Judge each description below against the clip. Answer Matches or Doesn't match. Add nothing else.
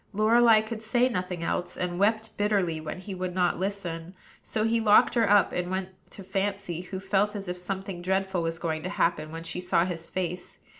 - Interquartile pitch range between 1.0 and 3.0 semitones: Matches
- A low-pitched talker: Doesn't match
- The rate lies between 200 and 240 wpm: Matches